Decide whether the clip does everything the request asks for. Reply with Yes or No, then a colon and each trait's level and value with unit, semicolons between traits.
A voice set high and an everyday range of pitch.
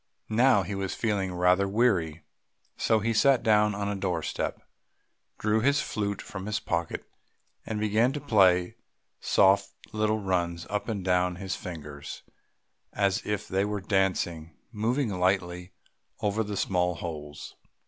No: low, 100 Hz; average, 3.0 semitones